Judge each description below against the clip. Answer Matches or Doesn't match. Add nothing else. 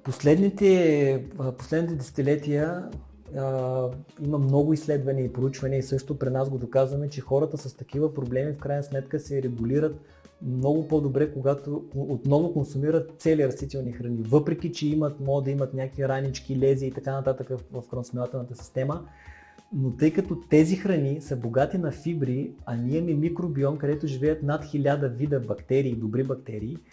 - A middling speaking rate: Matches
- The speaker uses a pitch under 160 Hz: Matches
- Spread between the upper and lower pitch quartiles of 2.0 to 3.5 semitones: Matches